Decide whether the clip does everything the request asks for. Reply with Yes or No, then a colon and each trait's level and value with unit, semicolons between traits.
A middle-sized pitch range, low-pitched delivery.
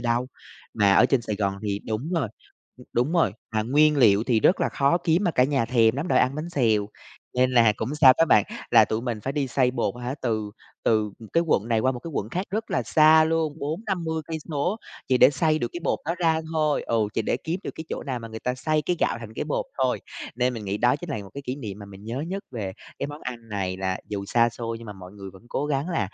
No: wide, 5.9 semitones; low, 125 Hz